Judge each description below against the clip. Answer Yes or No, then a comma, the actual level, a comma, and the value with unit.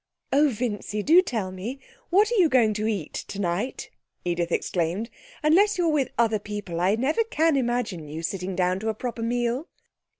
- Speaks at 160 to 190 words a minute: Yes, average, 175 wpm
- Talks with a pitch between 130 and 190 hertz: No, high, 220 Hz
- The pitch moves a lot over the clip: Yes, wide, 5.9 semitones